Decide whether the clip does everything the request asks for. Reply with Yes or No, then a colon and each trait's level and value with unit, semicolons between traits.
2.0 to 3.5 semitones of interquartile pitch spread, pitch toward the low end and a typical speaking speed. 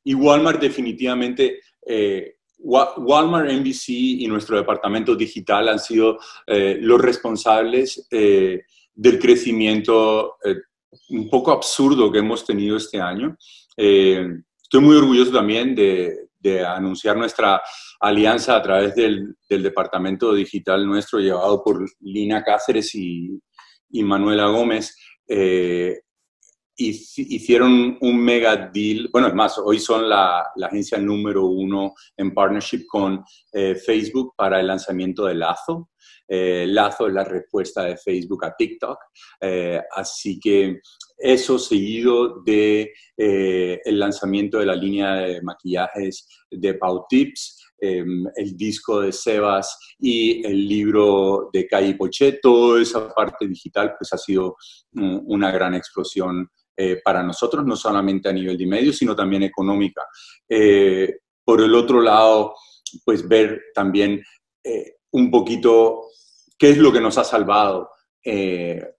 No: average, 4.3 semitones; low, 105 Hz; average, 135 wpm